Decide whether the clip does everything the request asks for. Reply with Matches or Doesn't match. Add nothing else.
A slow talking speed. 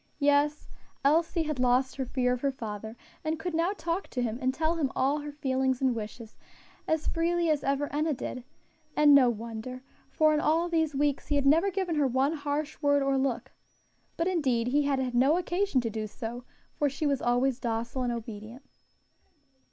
Doesn't match